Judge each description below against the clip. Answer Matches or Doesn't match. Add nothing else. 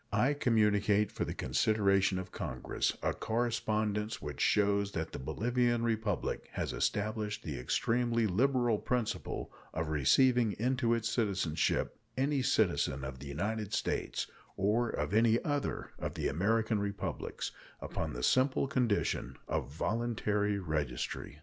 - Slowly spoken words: Matches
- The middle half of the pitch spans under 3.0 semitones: Doesn't match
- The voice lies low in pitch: Matches